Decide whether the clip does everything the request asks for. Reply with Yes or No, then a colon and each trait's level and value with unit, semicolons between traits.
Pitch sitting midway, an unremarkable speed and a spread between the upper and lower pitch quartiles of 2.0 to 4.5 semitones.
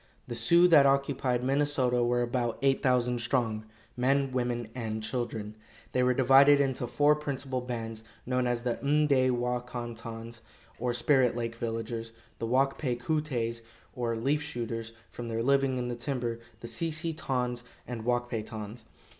No: low, 125 Hz; average, 170 wpm; narrow, 2.6 semitones